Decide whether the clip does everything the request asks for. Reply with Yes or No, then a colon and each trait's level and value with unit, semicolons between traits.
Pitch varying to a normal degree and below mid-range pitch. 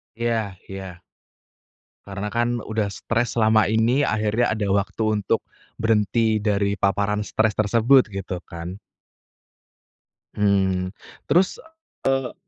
No: narrow, 2.3 semitones; low, 105 Hz